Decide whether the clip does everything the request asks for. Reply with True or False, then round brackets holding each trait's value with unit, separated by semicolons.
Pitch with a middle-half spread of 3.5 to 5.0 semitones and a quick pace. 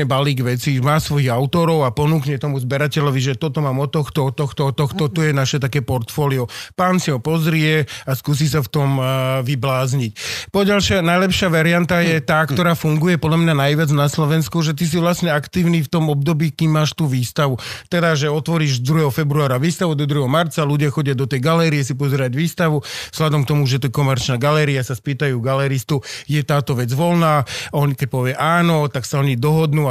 False (2.8 semitones; 195 wpm)